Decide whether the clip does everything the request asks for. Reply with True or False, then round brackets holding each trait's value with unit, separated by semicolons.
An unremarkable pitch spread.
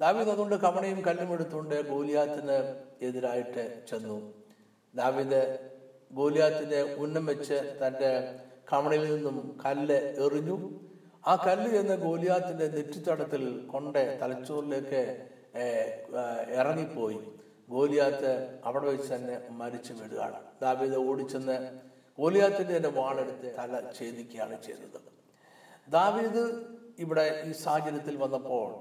True (3.3 semitones)